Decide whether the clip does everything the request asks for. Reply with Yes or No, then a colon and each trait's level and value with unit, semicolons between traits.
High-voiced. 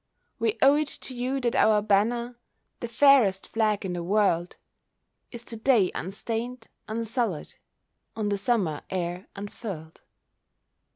Yes: high, 220 Hz